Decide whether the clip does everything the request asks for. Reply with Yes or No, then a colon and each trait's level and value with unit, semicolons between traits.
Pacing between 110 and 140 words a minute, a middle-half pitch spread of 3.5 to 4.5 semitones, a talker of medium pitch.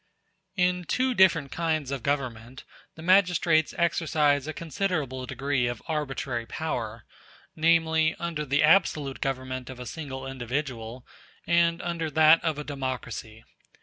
Yes: slow, 135 wpm; average, 4.1 semitones; medium, 150 Hz